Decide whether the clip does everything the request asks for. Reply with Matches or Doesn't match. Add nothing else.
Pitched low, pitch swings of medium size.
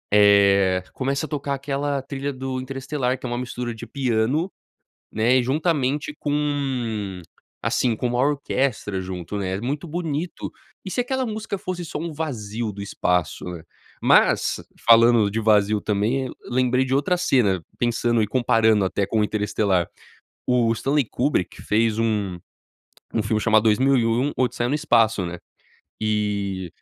Matches